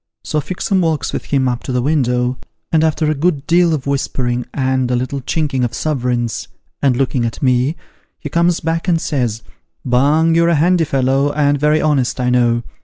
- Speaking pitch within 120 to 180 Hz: Yes, medium, 140 Hz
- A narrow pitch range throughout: No, average, 4.0 semitones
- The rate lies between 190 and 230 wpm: Yes, average, 195 wpm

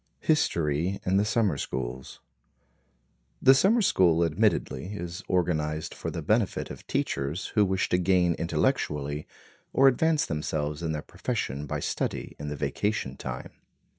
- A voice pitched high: No, very low, 85 Hz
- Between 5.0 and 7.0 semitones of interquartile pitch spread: Yes, wide, 5.4 semitones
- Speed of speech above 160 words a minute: No, average, 140 wpm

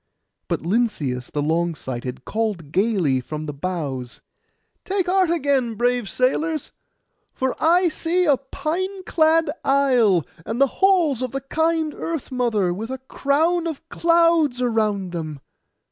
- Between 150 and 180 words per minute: No, average, 140 wpm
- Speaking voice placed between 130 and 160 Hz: No, very high, 250 Hz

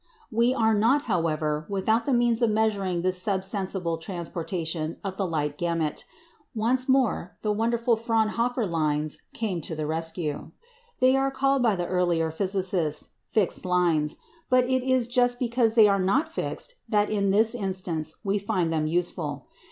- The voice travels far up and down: Yes, wide, 5.7 semitones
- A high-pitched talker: Yes, high, 195 Hz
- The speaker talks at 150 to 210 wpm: Yes, average, 160 wpm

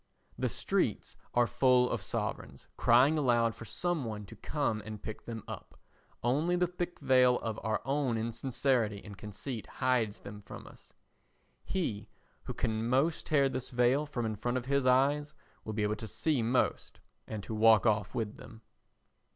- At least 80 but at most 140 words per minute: No, average, 175 wpm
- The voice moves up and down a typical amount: Yes, average, 3.8 semitones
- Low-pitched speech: Yes, low, 120 Hz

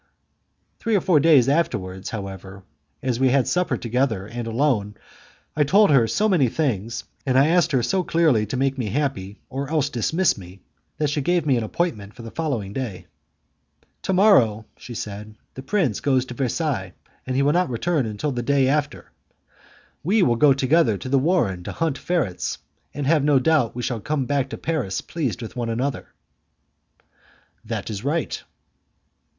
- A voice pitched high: No, low, 130 Hz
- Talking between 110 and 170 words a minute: No, average, 180 wpm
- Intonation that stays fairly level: No, average, 5.2 semitones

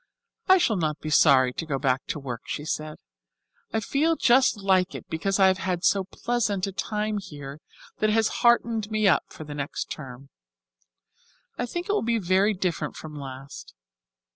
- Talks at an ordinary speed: Yes, average, 185 wpm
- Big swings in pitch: Yes, wide, 6.6 semitones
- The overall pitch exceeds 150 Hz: Yes, medium, 185 Hz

